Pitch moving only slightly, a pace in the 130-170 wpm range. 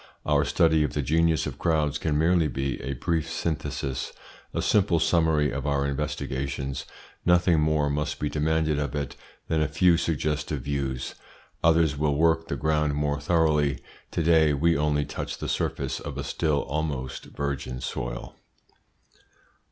Yes: narrow, 2.1 semitones; average, 155 wpm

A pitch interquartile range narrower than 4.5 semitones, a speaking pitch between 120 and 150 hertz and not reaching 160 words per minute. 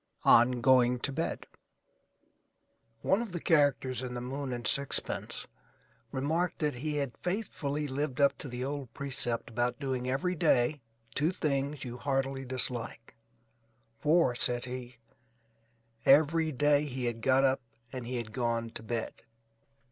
Yes: average, 3.0 semitones; low, 135 Hz; average, 145 wpm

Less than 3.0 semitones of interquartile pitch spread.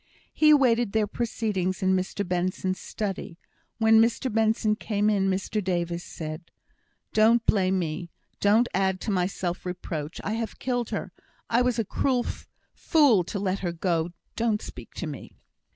No: average, 3.6 semitones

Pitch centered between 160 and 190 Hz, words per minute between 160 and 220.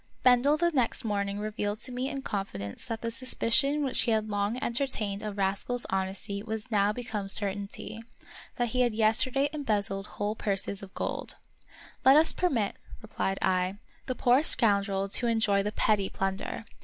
No: high, 215 Hz; average, 170 wpm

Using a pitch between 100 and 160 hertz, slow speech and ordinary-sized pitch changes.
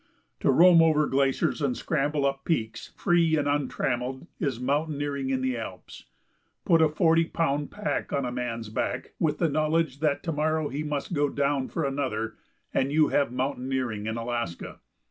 No: medium, 140 Hz; average, 170 wpm; average, 3.3 semitones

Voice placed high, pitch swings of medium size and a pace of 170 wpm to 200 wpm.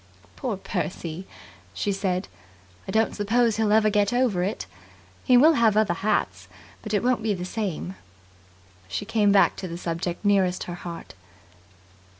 No: high, 205 Hz; average, 3.6 semitones; average, 160 wpm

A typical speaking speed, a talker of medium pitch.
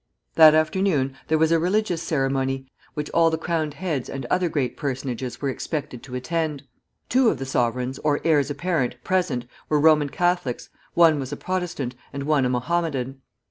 Yes: average, 175 wpm; medium, 150 Hz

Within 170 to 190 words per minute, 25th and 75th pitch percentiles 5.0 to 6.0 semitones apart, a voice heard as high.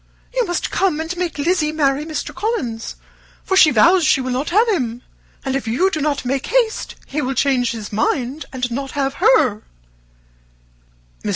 Yes: average, 180 wpm; average, 5.3 semitones; very high, 280 Hz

